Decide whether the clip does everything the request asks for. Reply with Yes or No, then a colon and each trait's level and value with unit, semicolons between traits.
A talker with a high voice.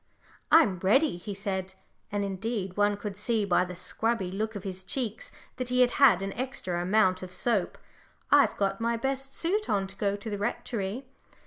Yes: high, 205 Hz